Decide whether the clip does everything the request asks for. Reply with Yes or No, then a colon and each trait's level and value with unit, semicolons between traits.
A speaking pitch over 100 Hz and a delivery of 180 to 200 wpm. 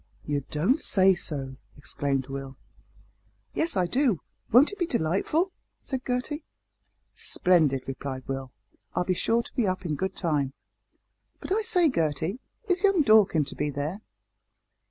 No: medium, 185 Hz; average, 150 wpm